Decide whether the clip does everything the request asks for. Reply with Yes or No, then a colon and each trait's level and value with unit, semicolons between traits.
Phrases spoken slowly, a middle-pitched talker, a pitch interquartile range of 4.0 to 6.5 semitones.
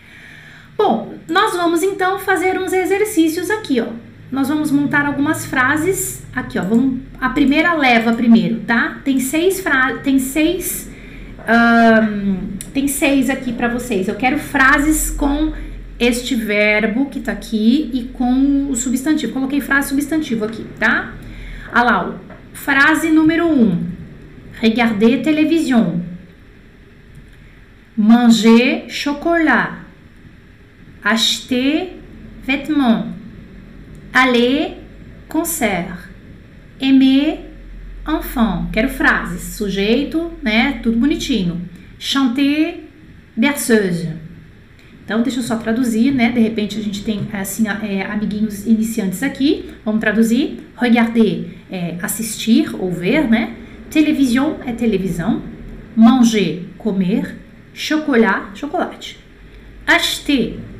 No: slow, 105 wpm; high, 245 Hz; average, 5.2 semitones